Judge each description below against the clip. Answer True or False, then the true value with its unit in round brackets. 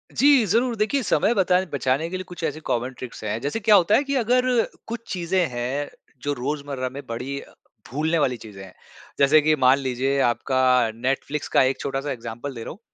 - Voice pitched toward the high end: False (140 Hz)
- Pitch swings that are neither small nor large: False (6.4 semitones)